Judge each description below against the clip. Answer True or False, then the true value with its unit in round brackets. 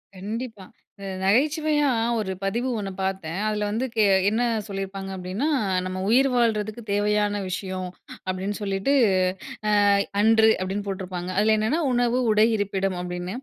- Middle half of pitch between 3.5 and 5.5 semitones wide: False (2.8 semitones)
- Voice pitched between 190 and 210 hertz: True (205 Hz)